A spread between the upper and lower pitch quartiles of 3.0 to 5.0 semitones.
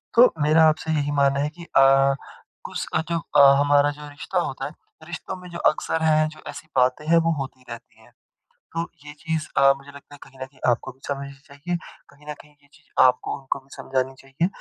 No: narrow, 2.4 semitones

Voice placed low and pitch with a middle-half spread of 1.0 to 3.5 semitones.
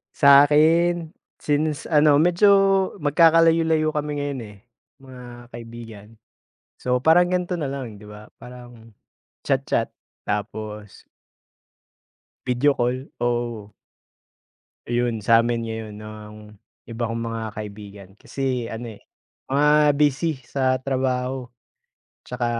No: low, 125 Hz; average, 4.5 semitones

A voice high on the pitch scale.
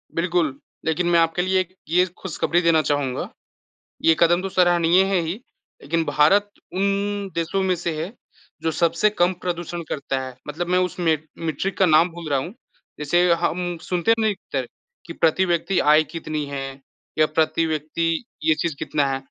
No: medium, 170 Hz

